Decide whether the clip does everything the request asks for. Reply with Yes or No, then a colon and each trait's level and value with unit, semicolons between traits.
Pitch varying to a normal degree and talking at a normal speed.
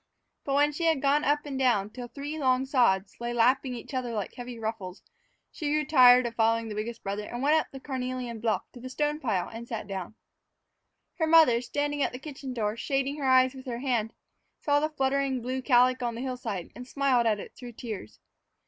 No: average, 3.3 semitones; fast, 215 wpm